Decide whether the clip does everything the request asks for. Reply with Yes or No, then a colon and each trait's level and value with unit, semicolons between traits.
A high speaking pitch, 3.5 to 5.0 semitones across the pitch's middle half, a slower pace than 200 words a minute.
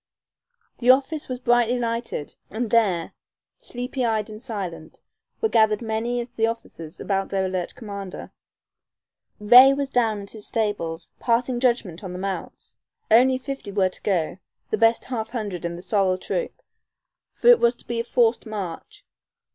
Yes: high, 225 Hz; average, 4.0 semitones; average, 165 wpm